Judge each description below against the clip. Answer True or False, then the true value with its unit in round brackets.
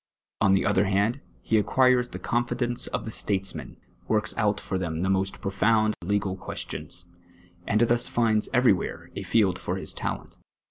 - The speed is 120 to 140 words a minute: False (165 wpm)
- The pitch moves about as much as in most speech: True (3.6 semitones)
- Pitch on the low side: True (105 Hz)